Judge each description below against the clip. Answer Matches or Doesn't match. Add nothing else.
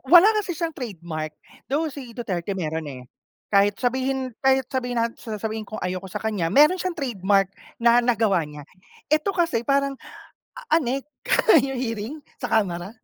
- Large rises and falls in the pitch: Matches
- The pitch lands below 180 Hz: Doesn't match